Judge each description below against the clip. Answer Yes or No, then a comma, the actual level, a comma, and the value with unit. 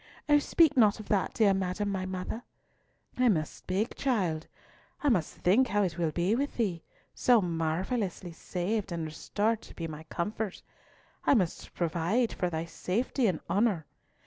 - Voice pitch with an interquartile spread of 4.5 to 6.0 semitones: Yes, average, 4.8 semitones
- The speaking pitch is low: No, high, 190 Hz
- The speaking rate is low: No, average, 165 wpm